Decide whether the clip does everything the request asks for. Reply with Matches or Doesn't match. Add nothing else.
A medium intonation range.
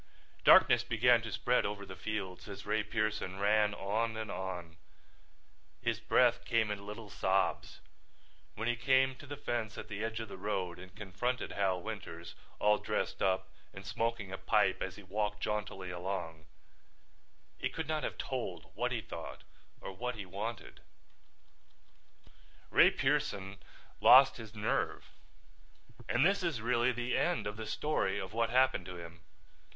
Matches